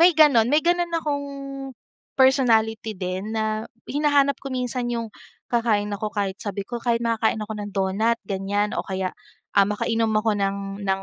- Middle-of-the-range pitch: No, high, 220 Hz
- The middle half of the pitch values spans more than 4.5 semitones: No, average, 3.9 semitones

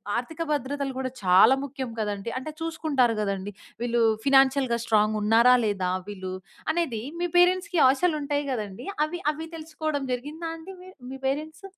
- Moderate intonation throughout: No, wide, 5.8 semitones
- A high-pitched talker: Yes, very high, 270 Hz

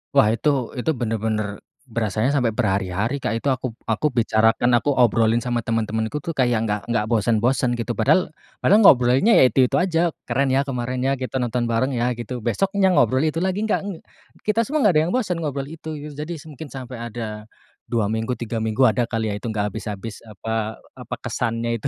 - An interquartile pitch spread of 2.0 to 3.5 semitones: No, average, 4.1 semitones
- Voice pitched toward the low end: Yes, low, 120 Hz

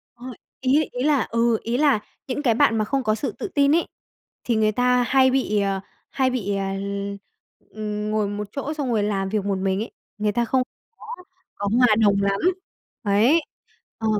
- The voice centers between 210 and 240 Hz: Yes, high, 225 Hz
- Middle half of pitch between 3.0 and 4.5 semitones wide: Yes, average, 4.1 semitones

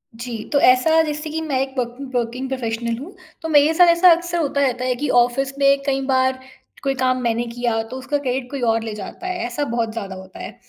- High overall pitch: Yes, very high, 260 Hz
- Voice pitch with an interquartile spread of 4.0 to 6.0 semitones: No, average, 3.4 semitones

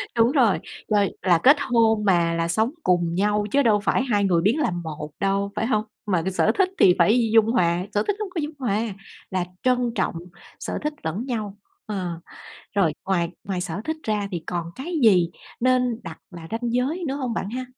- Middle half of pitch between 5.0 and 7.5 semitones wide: Yes, wide, 5.6 semitones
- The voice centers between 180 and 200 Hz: No, high, 210 Hz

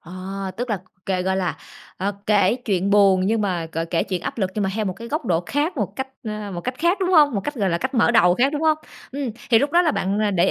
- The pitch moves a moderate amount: No, wide, 5.9 semitones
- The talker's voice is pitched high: Yes, high, 210 Hz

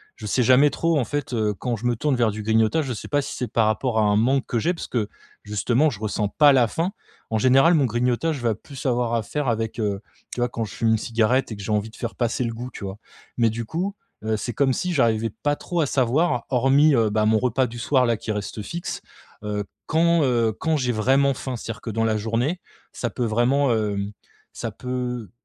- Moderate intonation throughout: Yes, average, 3.6 semitones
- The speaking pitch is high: No, low, 120 Hz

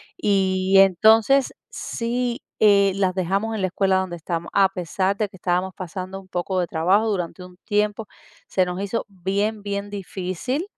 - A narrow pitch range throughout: Yes, narrow, 2.1 semitones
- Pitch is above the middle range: Yes, high, 195 Hz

